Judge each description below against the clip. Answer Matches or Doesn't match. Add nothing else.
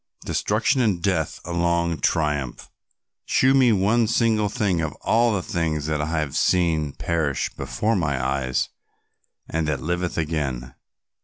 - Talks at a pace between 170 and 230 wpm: Doesn't match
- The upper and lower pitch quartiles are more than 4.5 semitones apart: Matches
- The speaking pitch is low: Matches